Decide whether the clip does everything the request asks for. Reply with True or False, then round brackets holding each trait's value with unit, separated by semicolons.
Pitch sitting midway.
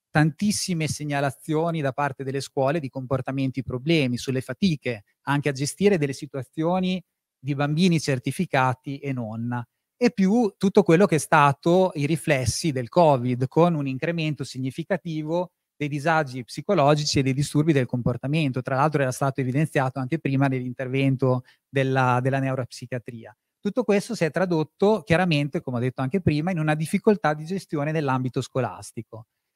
True (145 Hz)